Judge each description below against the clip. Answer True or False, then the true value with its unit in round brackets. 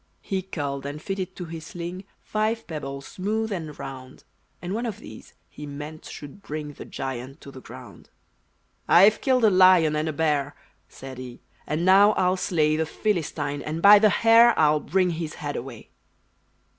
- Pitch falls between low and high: True (160 Hz)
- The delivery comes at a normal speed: True (175 wpm)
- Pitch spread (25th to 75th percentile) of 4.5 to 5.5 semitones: True (4.9 semitones)